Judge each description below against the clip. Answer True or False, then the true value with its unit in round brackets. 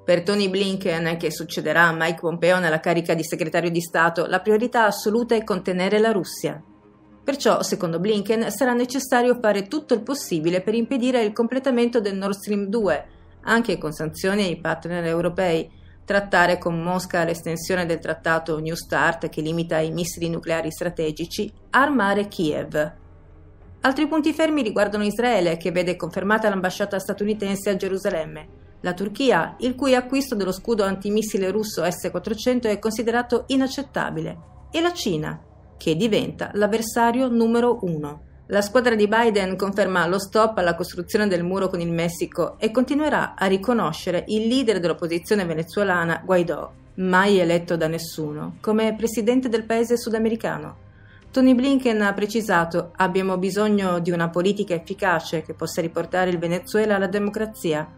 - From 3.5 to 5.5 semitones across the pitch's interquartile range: True (4.7 semitones)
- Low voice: False (195 Hz)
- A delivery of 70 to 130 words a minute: False (145 wpm)